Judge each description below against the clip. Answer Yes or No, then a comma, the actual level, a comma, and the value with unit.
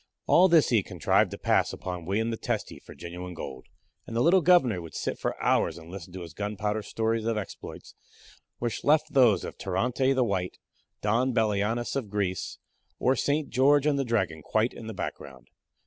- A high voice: No, low, 110 Hz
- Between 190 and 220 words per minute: Yes, average, 195 wpm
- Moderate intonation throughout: No, wide, 5.9 semitones